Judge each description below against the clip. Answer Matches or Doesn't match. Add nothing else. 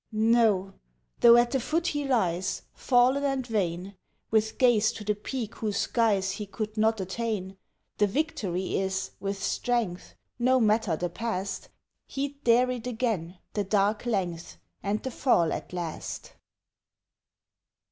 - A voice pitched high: Matches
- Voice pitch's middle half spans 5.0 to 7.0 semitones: Doesn't match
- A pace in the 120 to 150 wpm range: Matches